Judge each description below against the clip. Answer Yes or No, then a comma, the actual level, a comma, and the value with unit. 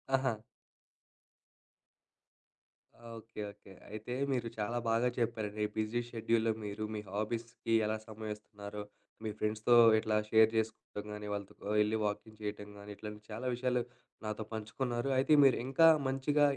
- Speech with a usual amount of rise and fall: No, narrow, 2.1 semitones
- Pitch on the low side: Yes, low, 110 Hz